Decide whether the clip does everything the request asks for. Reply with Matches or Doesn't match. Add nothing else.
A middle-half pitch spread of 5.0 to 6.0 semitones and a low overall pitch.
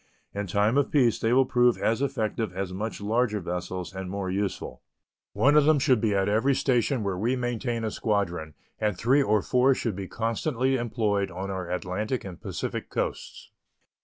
Doesn't match